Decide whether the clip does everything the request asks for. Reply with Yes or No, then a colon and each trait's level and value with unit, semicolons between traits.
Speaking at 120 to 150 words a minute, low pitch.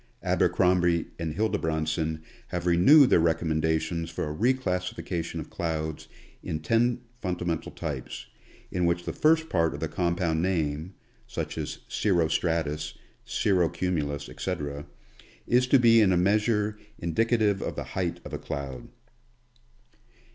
Yes: average, 140 wpm; very low, 85 Hz